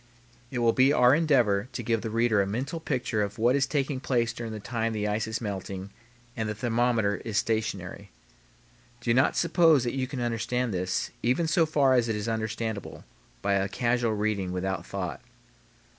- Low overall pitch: Yes, low, 115 Hz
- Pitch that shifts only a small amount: No, average, 3.2 semitones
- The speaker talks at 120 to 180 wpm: No, average, 190 wpm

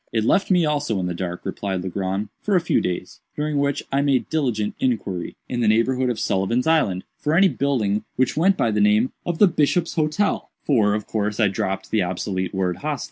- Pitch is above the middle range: No, low, 115 Hz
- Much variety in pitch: Yes, wide, 7.0 semitones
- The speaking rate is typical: No, fast, 210 wpm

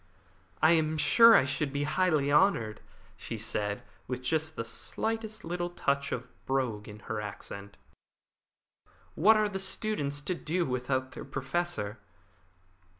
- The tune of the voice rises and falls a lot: Yes, wide, 5.8 semitones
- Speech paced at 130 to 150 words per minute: Yes, average, 140 wpm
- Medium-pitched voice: Yes, medium, 145 Hz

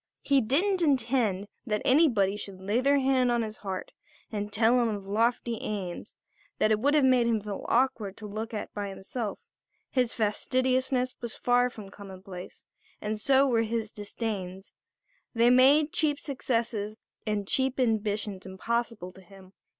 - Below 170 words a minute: Yes, average, 160 wpm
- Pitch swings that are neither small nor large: Yes, average, 3.8 semitones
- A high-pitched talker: Yes, high, 225 Hz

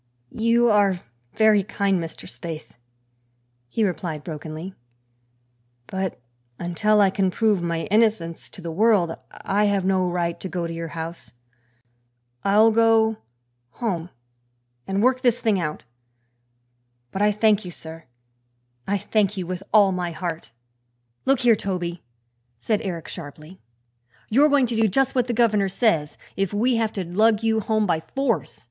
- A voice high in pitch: Yes, high, 195 Hz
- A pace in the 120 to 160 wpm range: Yes, average, 150 wpm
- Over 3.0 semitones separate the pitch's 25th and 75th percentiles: Yes, average, 4.3 semitones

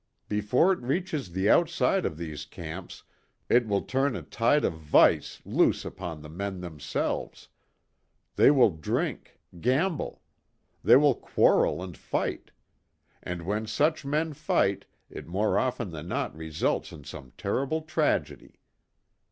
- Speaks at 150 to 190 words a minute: No, slow, 135 wpm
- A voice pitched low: Yes, low, 105 Hz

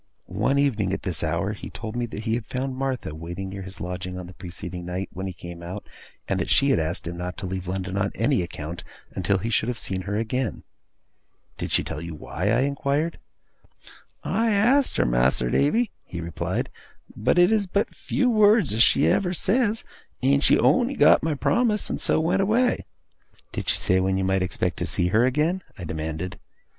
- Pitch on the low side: Yes, low, 105 Hz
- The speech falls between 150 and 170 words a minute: No, fast, 205 wpm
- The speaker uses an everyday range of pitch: No, wide, 8.4 semitones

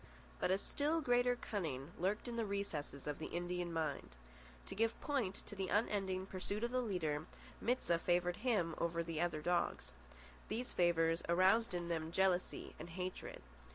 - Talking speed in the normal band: Yes, average, 165 wpm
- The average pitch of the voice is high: No, medium, 180 Hz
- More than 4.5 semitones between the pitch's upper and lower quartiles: No, average, 4.0 semitones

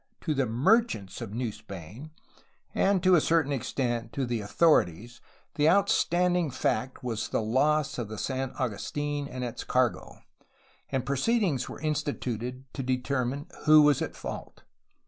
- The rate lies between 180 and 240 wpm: No, average, 150 wpm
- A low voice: Yes, low, 130 Hz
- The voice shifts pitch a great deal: No, average, 4.2 semitones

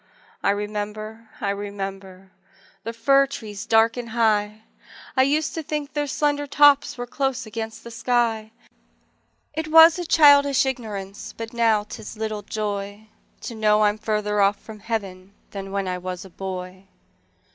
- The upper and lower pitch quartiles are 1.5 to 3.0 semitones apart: No, average, 4.0 semitones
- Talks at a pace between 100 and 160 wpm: Yes, average, 155 wpm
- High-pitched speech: Yes, high, 220 Hz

